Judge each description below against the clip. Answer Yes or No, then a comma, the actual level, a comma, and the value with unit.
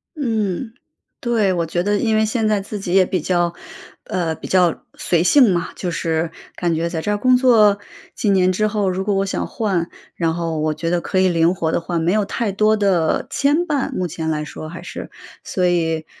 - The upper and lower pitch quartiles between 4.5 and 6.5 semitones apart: No, average, 3.9 semitones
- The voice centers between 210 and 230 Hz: No, medium, 185 Hz